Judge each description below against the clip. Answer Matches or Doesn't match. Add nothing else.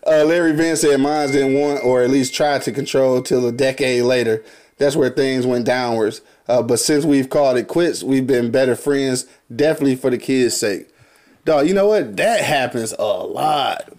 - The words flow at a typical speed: Matches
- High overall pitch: Doesn't match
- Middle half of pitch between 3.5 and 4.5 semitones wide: Doesn't match